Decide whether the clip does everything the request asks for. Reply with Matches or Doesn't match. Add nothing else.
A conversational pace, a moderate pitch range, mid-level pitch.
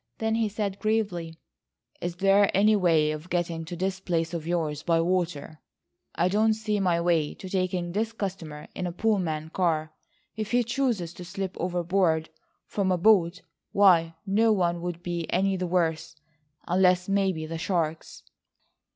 Matches